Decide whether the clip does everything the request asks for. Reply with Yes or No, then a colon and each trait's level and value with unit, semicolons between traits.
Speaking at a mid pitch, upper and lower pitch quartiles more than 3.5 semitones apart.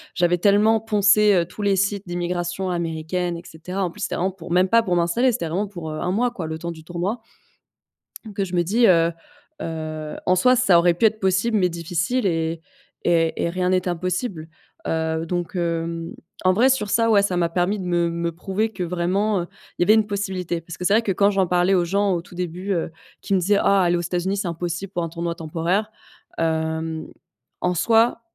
No: medium, 180 Hz; average, 2.9 semitones